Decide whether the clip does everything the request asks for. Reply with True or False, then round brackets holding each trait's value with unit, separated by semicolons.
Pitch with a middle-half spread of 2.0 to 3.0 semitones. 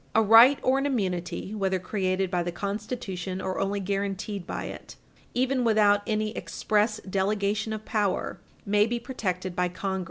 True (2.5 semitones)